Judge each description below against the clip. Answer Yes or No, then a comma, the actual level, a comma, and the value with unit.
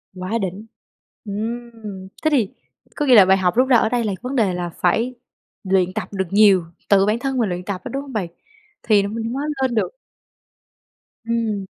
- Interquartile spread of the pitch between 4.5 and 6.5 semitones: No, average, 3.8 semitones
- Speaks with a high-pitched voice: Yes, high, 215 Hz